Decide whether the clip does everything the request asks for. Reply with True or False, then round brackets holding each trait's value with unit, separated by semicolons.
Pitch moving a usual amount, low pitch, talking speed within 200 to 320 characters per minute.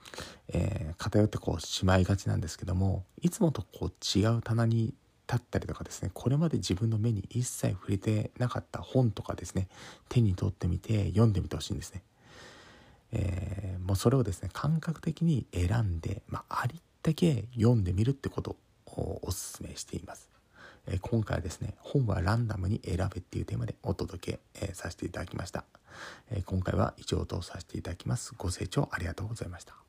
False (4.1 semitones; 105 Hz; 385 characters per minute)